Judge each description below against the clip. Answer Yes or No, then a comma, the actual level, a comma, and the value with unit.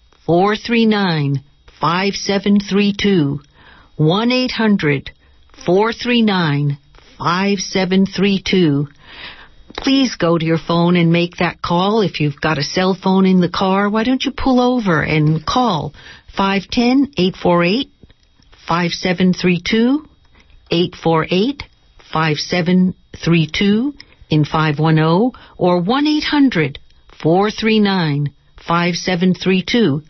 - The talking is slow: Yes, slow, 70 wpm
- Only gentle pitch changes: No, average, 4.4 semitones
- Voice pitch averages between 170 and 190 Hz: Yes, medium, 185 Hz